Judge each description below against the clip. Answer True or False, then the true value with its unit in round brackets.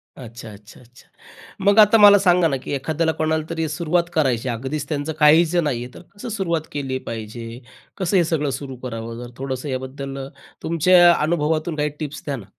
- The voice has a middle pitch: True (150 Hz)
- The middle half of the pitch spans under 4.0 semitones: False (4.5 semitones)